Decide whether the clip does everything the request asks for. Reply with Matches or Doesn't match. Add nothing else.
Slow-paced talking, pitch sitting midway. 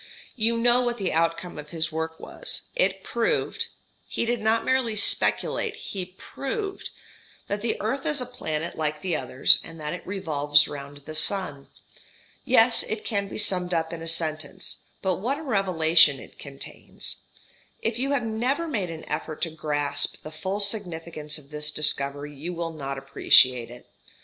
Doesn't match